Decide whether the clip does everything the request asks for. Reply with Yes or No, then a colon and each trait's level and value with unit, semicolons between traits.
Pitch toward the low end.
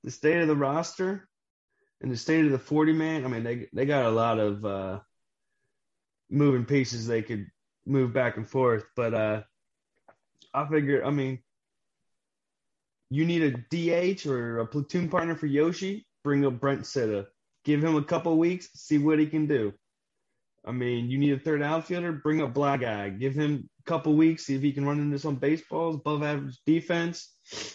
No: medium, 145 Hz